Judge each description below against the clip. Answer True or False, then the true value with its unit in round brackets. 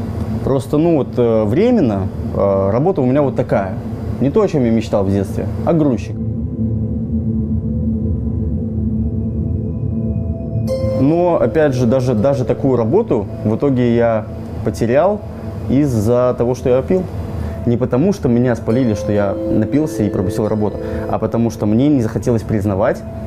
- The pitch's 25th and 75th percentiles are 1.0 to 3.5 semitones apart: True (2.4 semitones)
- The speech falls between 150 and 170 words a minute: False (135 wpm)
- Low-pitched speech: True (110 Hz)